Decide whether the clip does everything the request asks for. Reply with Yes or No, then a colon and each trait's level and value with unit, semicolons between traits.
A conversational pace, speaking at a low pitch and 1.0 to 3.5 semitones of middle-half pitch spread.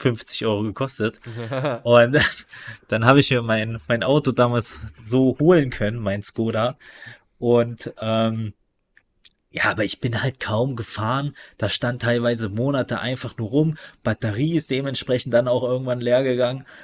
Yes: average, 145 wpm; low, 120 Hz; narrow, 2.6 semitones